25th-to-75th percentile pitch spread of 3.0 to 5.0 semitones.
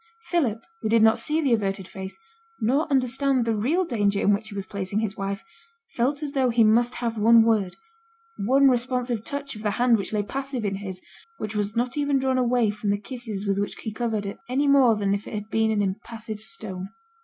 Yes: average, 3.6 semitones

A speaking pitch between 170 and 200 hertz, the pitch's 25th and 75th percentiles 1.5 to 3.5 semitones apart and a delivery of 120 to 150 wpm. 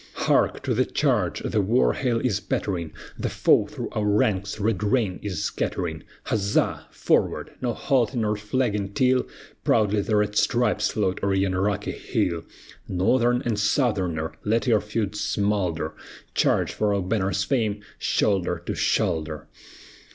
No: low, 105 Hz; average, 2.8 semitones; average, 145 wpm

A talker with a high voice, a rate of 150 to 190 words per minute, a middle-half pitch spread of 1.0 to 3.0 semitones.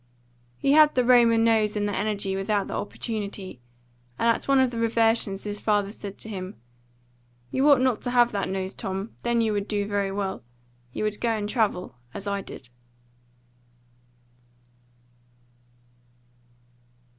Yes: high, 210 Hz; average, 155 wpm; narrow, 2.6 semitones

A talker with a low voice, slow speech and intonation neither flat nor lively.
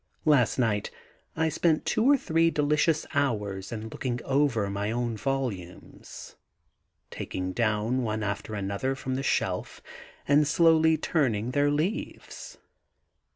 No: low, 130 Hz; slow, 125 wpm; wide, 6.0 semitones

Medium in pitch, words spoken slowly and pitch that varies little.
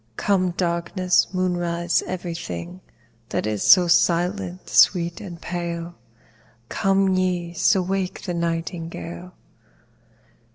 Yes: medium, 175 Hz; slow, 100 wpm; narrow, 1.5 semitones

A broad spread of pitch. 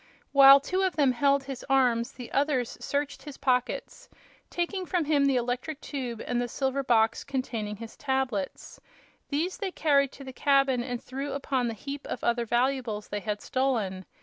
No: average, 2.9 semitones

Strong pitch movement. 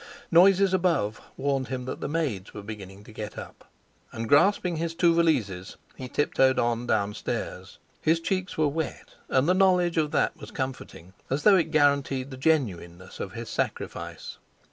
Yes: wide, 6.9 semitones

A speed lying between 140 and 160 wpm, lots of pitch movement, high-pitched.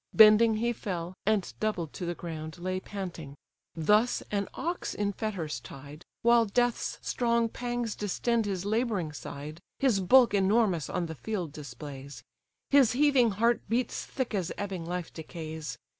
Yes: average, 150 wpm; wide, 6.0 semitones; high, 200 Hz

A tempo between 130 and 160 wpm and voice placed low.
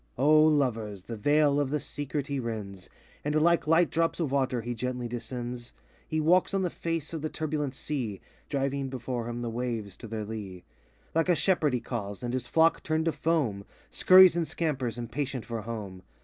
No: average, 190 wpm; low, 130 Hz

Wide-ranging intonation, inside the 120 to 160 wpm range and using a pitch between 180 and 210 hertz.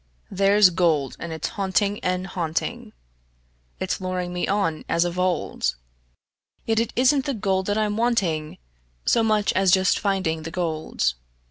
No: average, 3.5 semitones; average, 150 wpm; high, 190 Hz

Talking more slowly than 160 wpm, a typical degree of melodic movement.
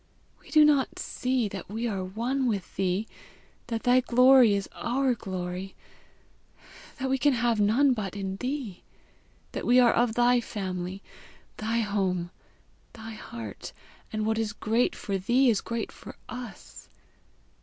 Yes: average, 150 wpm; average, 4.2 semitones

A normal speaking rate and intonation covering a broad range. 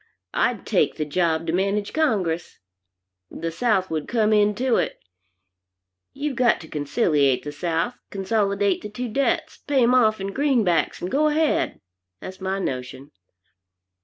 Yes: average, 145 wpm; wide, 6.7 semitones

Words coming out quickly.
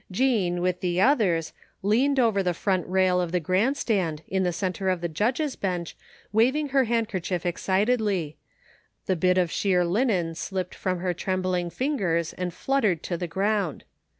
No: average, 165 wpm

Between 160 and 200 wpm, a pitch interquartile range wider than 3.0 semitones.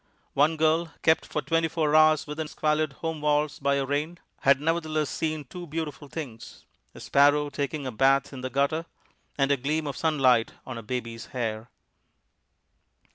No: average, 170 wpm; narrow, 2.6 semitones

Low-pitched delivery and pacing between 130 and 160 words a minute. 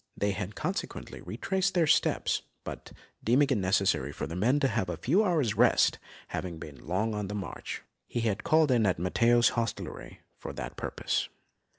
No: low, 110 Hz; average, 180 wpm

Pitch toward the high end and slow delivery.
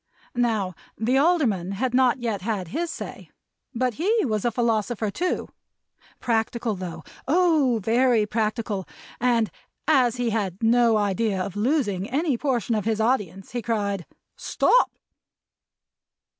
Yes: high, 230 Hz; slow, 130 wpm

